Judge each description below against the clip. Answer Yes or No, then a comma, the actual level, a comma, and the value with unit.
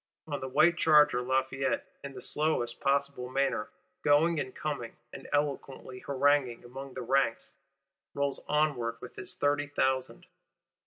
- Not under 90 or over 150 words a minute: Yes, average, 140 wpm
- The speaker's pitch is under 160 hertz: Yes, medium, 140 Hz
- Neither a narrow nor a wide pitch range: No, narrow, 2.2 semitones